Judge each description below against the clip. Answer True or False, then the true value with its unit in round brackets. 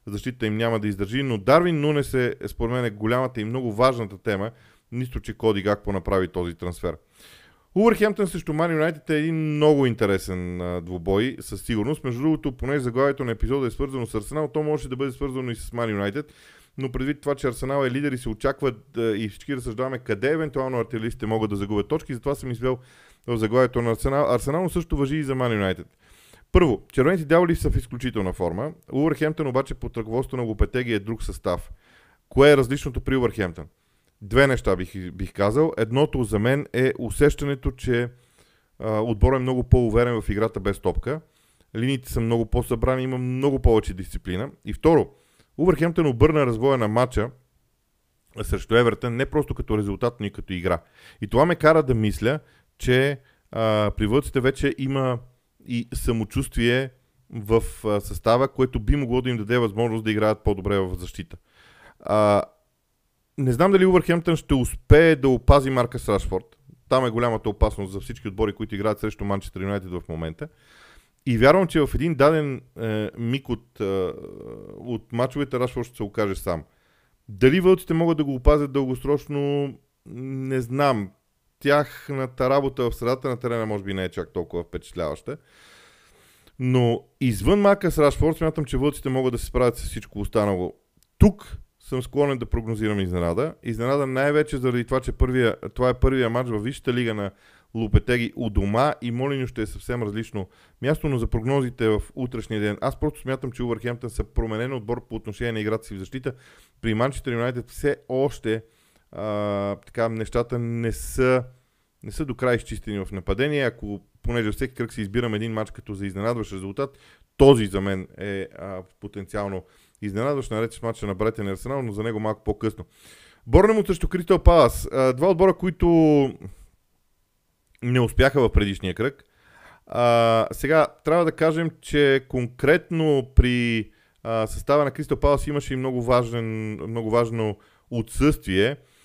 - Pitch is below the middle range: True (120 Hz)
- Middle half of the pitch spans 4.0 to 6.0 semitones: True (4.4 semitones)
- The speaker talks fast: True (170 wpm)